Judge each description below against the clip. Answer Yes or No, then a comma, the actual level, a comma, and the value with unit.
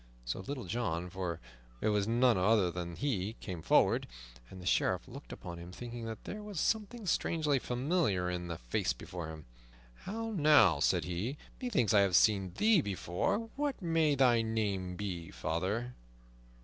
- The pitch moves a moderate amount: No, wide, 8.4 semitones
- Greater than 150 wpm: Yes, average, 165 wpm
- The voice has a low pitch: Yes, low, 105 Hz